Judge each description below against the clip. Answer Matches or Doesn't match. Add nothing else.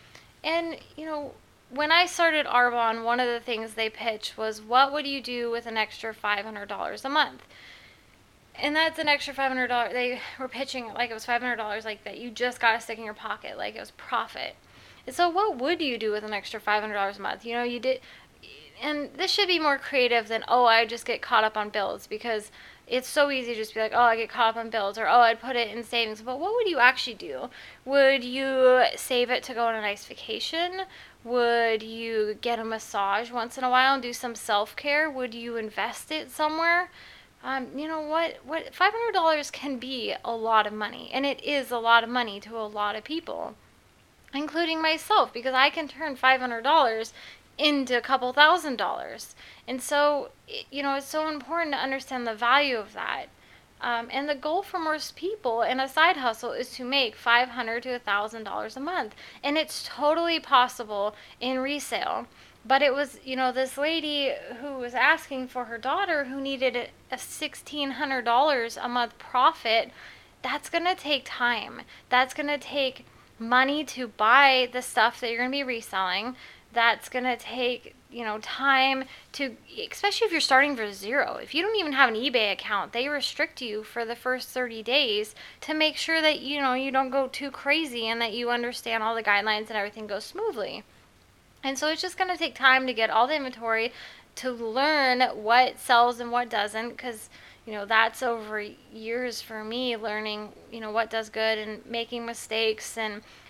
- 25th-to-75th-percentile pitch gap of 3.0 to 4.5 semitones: Matches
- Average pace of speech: Doesn't match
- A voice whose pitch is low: Doesn't match